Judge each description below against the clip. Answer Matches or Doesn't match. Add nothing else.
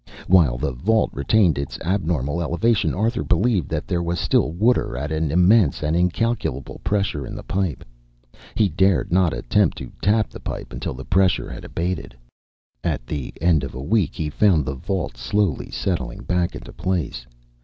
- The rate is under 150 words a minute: Doesn't match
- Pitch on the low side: Matches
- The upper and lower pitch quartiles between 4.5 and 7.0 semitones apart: Matches